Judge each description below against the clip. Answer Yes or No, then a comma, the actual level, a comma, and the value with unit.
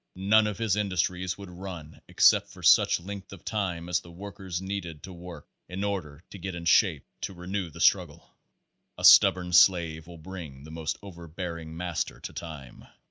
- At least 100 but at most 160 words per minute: No, average, 185 wpm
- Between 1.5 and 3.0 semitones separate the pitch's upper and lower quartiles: Yes, narrow, 2.6 semitones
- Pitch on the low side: Yes, very low, 90 Hz